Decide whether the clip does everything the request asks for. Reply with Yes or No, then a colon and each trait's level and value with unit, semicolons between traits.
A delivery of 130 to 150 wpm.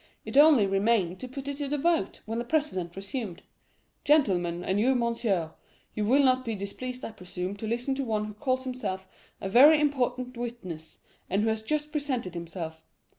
No: average, 180 wpm